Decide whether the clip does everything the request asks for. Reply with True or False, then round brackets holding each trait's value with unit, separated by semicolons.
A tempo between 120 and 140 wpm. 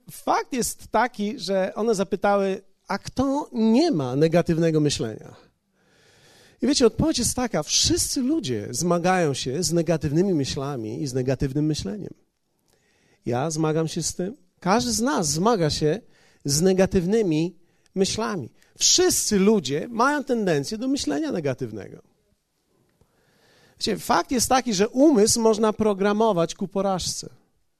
True (125 wpm)